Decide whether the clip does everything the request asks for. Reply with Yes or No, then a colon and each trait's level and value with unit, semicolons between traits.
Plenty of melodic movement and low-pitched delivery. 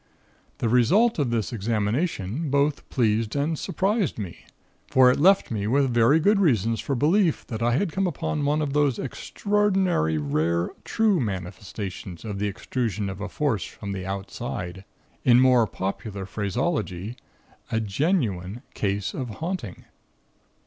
Yes: wide, 7.2 semitones; low, 120 Hz